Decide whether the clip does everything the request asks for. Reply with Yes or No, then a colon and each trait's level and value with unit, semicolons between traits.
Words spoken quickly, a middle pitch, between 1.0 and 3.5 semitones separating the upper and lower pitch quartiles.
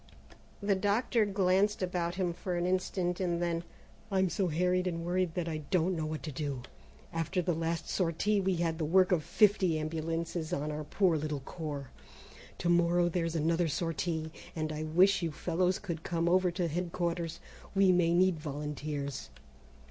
No: average, 170 wpm; medium, 170 Hz; narrow, 2.4 semitones